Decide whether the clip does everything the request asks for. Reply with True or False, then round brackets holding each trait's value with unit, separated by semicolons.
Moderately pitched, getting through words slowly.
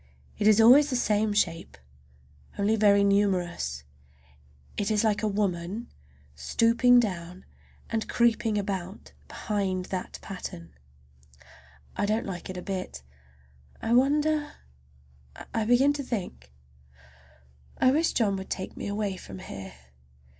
False (200 Hz; 125 wpm)